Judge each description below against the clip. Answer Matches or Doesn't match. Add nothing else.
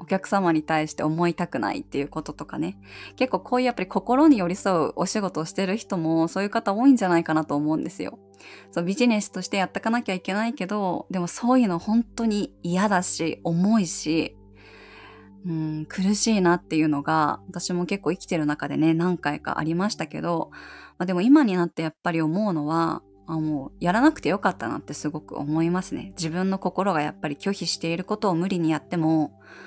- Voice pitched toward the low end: Doesn't match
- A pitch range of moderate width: Matches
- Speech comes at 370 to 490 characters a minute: Matches